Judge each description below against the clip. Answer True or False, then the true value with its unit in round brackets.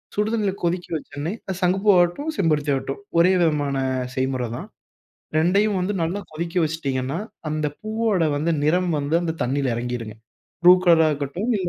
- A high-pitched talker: False (165 Hz)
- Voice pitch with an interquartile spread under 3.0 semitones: False (4.2 semitones)